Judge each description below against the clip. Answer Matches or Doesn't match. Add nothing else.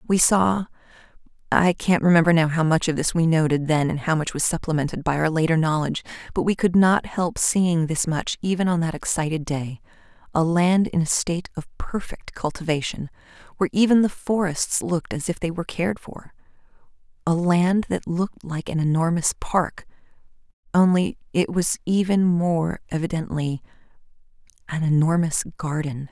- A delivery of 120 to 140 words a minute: Doesn't match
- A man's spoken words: Doesn't match